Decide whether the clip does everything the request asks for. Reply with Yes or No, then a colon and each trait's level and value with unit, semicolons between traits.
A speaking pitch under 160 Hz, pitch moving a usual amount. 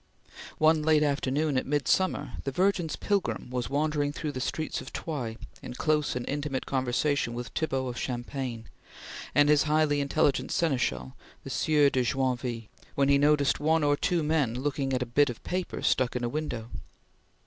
Yes: medium, 140 Hz; average, 3.2 semitones